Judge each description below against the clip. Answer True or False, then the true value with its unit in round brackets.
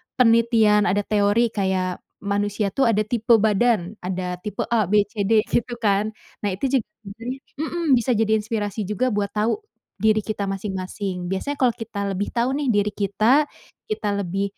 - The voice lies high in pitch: True (210 Hz)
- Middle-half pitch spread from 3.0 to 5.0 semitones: False (2.6 semitones)